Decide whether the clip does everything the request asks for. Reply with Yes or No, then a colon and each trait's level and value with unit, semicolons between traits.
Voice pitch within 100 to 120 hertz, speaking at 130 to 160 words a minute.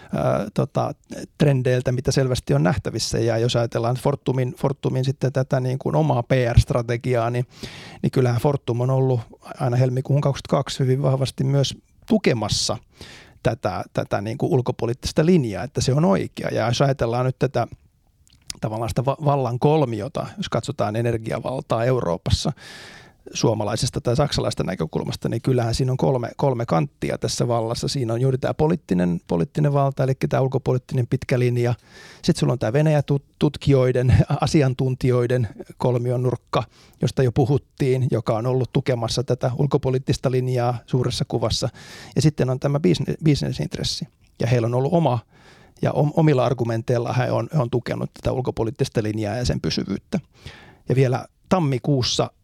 No: low, 130 Hz; average, 145 wpm